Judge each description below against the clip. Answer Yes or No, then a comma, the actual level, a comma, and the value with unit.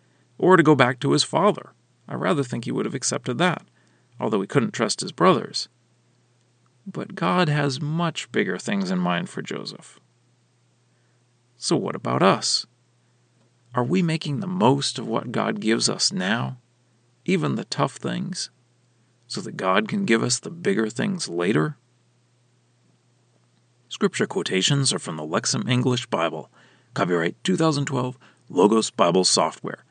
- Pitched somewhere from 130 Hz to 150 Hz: No, low, 120 Hz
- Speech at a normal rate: Yes, average, 145 wpm